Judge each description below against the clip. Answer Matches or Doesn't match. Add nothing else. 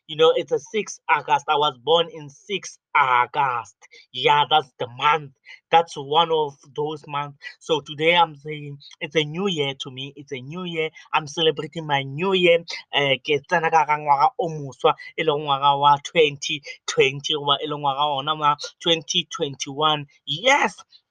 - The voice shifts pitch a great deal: Doesn't match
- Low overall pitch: Doesn't match